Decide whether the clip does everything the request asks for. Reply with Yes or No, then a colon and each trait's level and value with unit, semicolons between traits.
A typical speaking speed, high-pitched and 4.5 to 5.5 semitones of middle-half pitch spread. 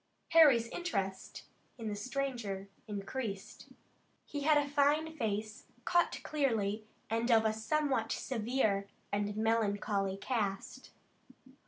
No: slow, 110 wpm; high, 225 Hz; average, 5.2 semitones